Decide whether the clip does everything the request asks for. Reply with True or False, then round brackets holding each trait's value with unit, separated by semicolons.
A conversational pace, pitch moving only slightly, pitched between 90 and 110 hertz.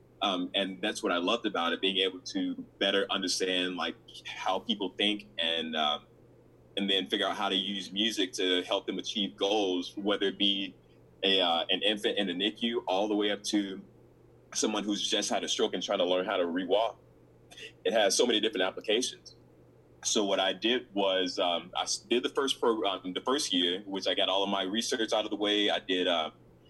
False (215 wpm; 2.0 semitones; 100 Hz)